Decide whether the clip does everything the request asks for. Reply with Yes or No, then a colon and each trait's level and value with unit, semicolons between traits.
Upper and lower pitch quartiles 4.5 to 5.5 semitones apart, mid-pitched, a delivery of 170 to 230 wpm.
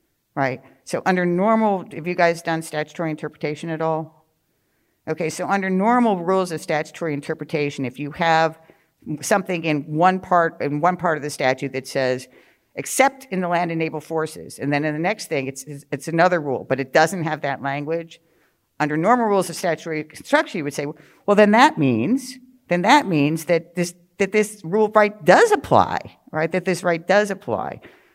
No: average, 3.7 semitones; medium, 165 Hz; average, 190 wpm